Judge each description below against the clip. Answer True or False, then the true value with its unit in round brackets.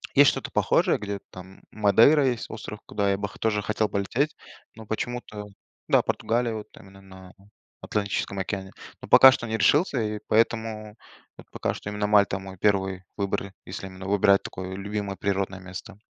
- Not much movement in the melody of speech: True (2.2 semitones)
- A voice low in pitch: True (100 Hz)